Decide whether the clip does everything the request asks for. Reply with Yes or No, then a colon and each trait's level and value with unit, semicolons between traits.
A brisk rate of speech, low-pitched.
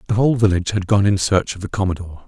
Yes: fast, 265 wpm; low, 100 Hz